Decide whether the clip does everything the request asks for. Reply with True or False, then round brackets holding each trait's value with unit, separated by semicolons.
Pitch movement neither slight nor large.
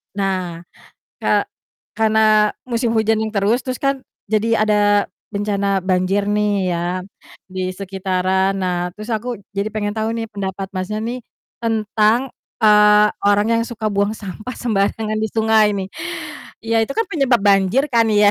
False (2.2 semitones)